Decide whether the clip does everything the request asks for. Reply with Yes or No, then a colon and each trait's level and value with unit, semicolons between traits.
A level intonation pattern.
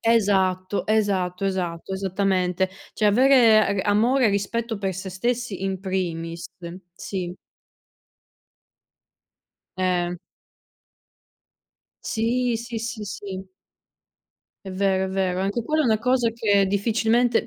No: average, 3.3 semitones